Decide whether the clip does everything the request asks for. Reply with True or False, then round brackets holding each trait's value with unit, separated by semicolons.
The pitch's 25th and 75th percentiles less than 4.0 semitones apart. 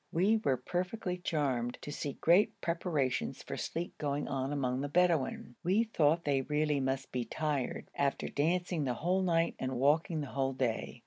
False (4.4 semitones)